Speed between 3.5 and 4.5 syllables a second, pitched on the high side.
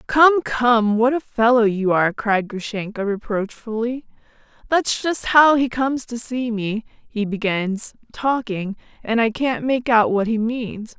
Yes: 4.1 syllables/s; high, 230 Hz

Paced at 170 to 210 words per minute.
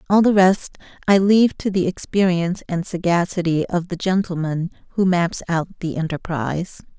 No: average, 155 wpm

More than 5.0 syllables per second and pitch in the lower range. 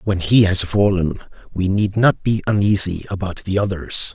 No: 4.6 syllables/s; low, 100 Hz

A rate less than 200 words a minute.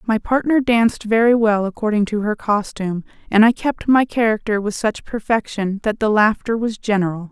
Yes: average, 180 wpm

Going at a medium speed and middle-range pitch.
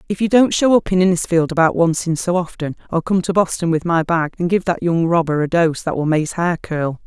No: fast, 270 wpm; medium, 170 Hz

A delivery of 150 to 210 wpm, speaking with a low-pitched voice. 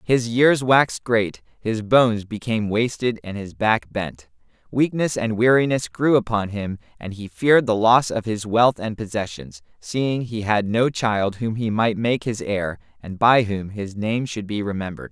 Yes: average, 185 wpm; low, 110 Hz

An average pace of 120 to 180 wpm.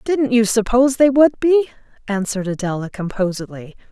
Yes: average, 140 wpm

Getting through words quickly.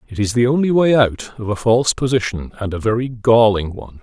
Yes: fast, 225 wpm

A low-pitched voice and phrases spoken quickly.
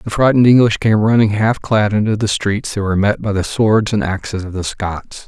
Yes: low, 105 Hz; fast, 250 wpm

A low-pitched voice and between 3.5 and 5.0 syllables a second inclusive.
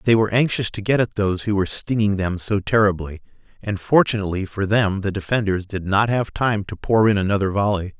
No: low, 100 Hz; 5.9 syllables/s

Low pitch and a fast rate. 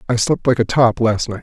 Yes: low, 115 Hz; fast, 295 wpm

